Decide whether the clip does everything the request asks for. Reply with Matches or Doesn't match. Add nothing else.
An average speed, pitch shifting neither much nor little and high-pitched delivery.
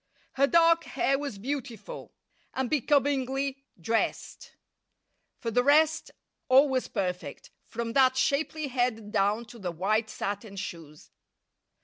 Doesn't match